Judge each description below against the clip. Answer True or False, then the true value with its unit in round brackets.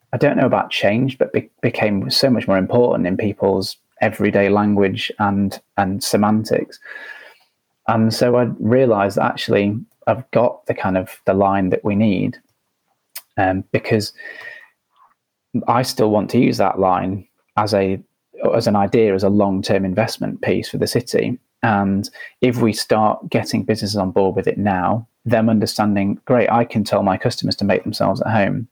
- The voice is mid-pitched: False (105 Hz)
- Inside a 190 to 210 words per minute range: False (170 wpm)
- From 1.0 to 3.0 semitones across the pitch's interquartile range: True (2.5 semitones)